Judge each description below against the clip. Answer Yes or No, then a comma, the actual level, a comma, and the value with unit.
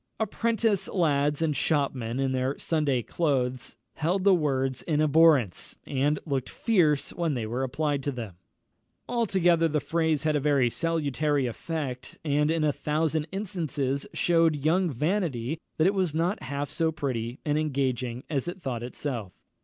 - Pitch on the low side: No, medium, 150 Hz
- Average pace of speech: Yes, average, 155 wpm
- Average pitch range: Yes, average, 3.8 semitones